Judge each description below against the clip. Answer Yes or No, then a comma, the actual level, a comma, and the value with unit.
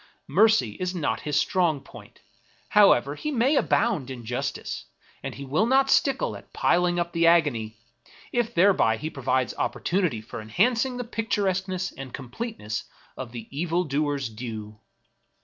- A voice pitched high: No, medium, 165 Hz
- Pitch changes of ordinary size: No, wide, 8.0 semitones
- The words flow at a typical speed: Yes, average, 150 wpm